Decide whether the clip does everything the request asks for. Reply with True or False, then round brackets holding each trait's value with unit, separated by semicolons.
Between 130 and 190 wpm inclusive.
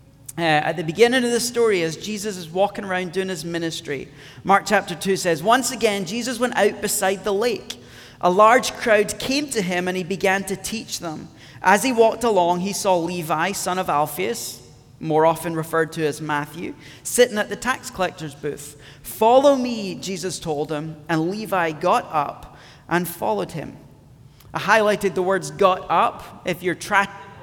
True (180 wpm)